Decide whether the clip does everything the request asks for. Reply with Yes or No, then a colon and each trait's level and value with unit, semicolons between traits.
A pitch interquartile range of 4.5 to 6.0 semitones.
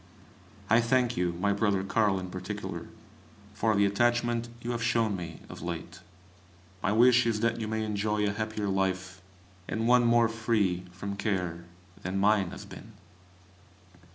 No: average, 3.4 semitones